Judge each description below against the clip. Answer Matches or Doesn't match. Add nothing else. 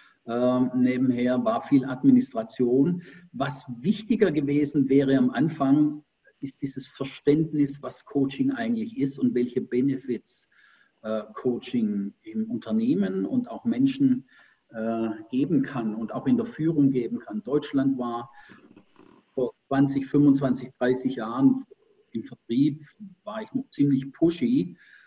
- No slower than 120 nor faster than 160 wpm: Matches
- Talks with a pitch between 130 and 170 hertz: Matches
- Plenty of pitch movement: Matches